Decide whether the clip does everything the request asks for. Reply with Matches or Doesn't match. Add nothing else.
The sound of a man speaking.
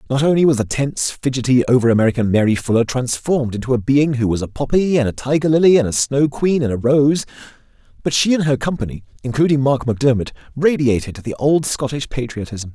Matches